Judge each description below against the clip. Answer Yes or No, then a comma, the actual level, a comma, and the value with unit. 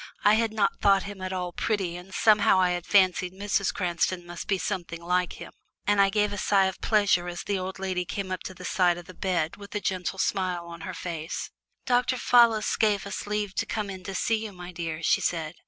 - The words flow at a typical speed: No, fast, 235 wpm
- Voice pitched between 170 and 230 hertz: Yes, high, 190 Hz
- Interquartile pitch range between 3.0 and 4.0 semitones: No, narrow, 2.5 semitones